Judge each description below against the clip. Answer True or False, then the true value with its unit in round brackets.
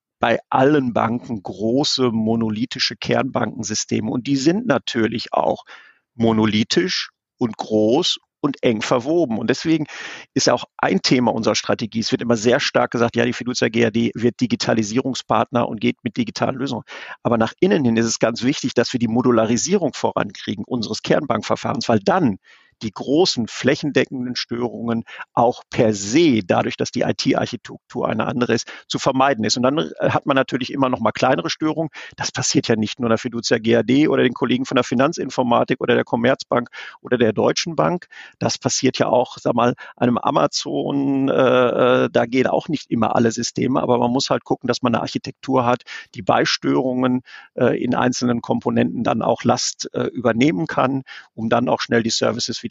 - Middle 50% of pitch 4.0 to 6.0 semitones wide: False (2.4 semitones)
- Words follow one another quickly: False (175 wpm)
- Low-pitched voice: True (120 Hz)